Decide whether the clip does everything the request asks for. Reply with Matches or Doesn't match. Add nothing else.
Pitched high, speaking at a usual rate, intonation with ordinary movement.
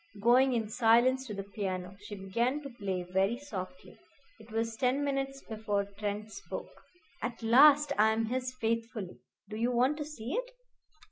Matches